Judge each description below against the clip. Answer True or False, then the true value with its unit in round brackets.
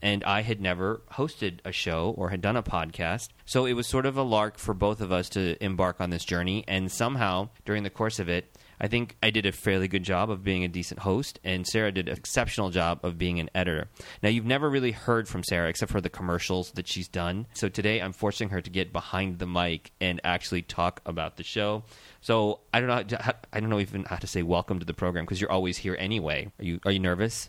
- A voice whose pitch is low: True (95 Hz)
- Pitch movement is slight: False (3.5 semitones)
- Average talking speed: False (255 wpm)